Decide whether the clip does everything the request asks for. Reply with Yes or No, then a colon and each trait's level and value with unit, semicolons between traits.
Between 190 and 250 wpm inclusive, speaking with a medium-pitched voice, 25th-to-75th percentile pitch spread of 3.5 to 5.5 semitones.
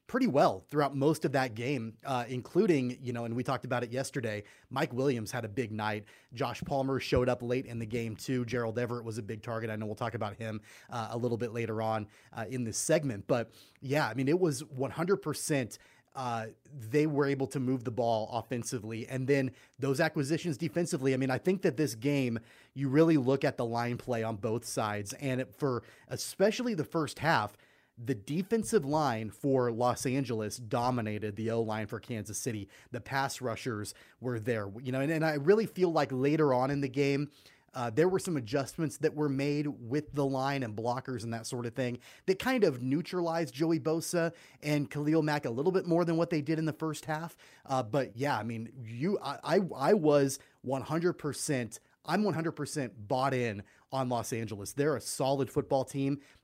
No: fast, 205 wpm; low, 130 Hz; average, 4.0 semitones